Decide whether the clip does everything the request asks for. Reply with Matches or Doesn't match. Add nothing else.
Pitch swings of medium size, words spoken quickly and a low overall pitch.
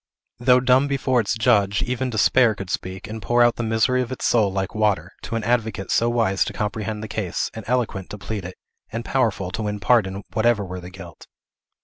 Matches